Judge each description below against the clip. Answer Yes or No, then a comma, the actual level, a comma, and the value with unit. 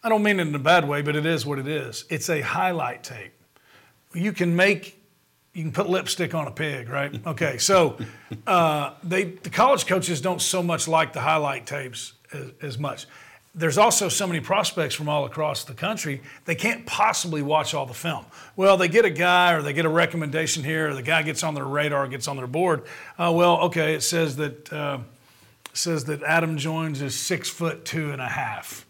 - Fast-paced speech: Yes, fast, 215 wpm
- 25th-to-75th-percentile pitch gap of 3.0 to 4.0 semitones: Yes, average, 3.4 semitones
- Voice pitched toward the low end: No, medium, 160 Hz